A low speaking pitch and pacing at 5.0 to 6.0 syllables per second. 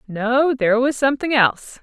No: very high, 250 Hz; 5.4 syllables/s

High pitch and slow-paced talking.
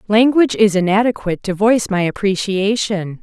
Yes: high, 205 Hz; slow, 130 wpm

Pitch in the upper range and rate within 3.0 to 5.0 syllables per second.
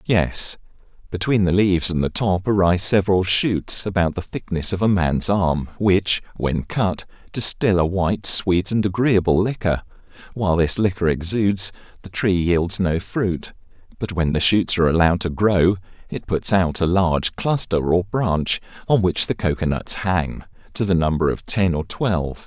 No: very low, 90 Hz; 4.7 syllables/s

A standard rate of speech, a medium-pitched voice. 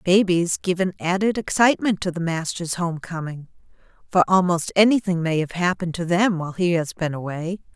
Yes: average, 170 wpm; medium, 175 Hz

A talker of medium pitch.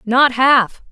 No: very high, 250 Hz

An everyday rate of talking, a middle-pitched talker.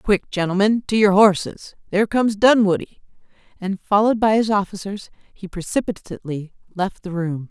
No: average, 145 wpm; high, 200 Hz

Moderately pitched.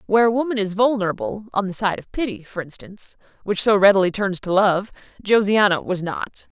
No: high, 200 Hz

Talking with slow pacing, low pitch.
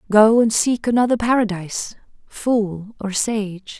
No: slow, 125 wpm; high, 215 Hz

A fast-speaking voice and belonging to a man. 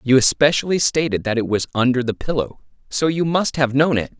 Yes: fast, 215 wpm; male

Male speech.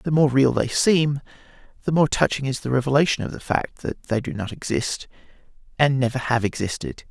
Yes: male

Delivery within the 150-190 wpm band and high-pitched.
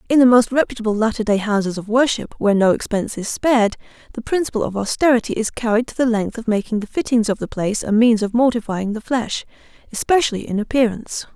No: fast, 205 wpm; high, 225 Hz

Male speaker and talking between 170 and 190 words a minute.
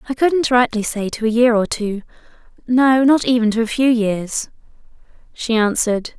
No: female; average, 175 wpm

